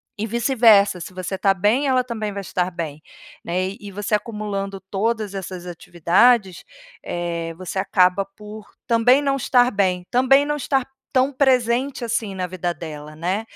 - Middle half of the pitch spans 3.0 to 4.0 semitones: No, average, 4.6 semitones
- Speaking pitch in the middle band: No, high, 200 Hz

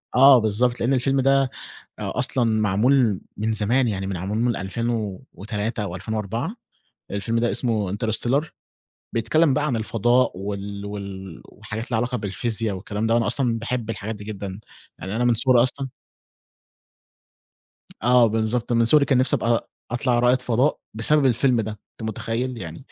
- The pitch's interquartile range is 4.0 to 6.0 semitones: No, average, 3.2 semitones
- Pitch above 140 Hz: No, low, 115 Hz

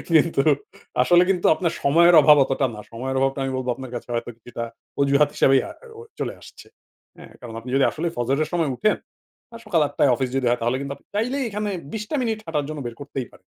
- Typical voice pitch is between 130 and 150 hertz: Yes, medium, 140 Hz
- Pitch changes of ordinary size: Yes, average, 5.0 semitones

